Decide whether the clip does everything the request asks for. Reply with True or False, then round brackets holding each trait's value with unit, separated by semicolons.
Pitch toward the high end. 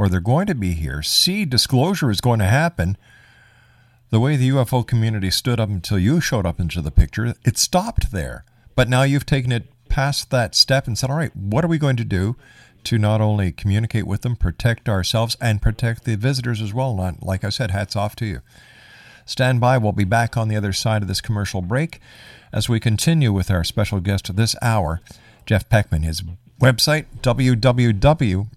False (115 Hz)